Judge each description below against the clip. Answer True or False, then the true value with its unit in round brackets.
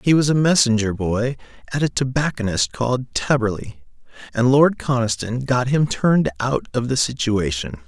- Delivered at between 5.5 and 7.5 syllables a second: False (5.1 syllables/s)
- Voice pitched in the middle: False (125 Hz)